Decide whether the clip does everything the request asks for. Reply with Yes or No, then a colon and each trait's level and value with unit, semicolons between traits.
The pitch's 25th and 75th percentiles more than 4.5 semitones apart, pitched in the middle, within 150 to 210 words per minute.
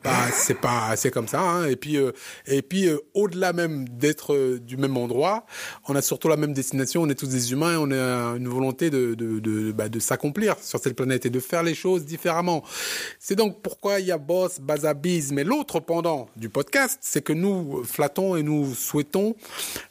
No: average, 5.2 semitones; medium, 150 Hz; fast, 220 wpm